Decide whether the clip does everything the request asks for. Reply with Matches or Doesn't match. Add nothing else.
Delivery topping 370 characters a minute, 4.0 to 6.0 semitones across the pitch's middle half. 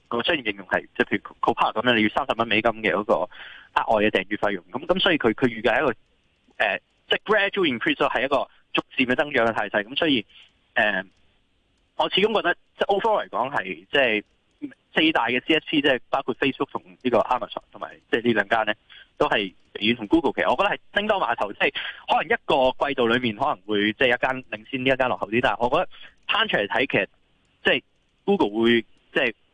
Matches